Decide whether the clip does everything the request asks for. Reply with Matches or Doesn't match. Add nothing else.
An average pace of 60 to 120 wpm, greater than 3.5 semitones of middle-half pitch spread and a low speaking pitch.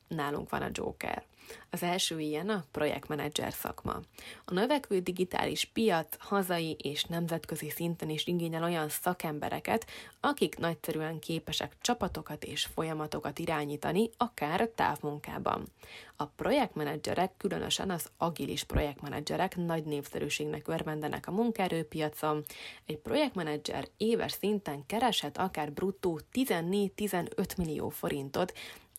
Doesn't match